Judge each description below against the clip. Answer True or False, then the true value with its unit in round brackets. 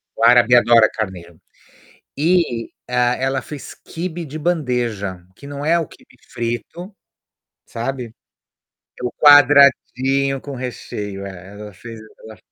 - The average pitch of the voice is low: True (125 Hz)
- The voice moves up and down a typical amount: True (4.3 semitones)